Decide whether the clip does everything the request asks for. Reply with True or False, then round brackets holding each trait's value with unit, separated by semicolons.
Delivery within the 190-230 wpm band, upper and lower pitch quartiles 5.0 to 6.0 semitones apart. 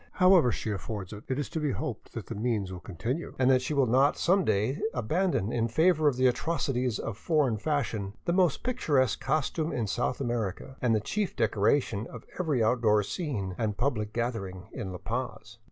True (195 wpm; 5.3 semitones)